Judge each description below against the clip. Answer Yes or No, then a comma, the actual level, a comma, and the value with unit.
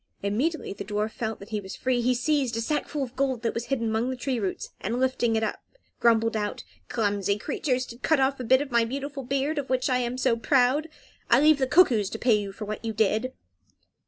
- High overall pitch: Yes, high, 245 Hz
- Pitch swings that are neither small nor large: Yes, average, 3.3 semitones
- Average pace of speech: No, fast, 235 wpm